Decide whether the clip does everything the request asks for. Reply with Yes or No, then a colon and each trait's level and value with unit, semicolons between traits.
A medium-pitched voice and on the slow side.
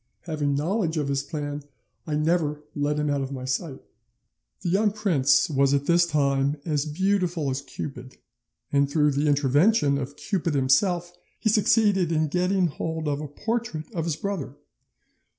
No: medium, 150 Hz; average, 165 wpm